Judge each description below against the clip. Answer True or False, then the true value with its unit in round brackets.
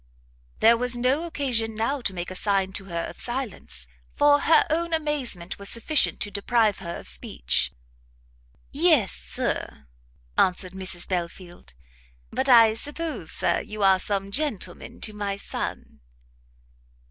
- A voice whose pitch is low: False (215 Hz)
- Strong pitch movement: True (6.3 semitones)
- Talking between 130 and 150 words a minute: True (140 wpm)